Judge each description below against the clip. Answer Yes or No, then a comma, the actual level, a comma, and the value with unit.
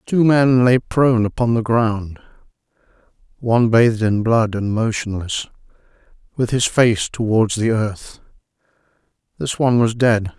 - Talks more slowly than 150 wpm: Yes, slow, 135 wpm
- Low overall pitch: Yes, low, 115 Hz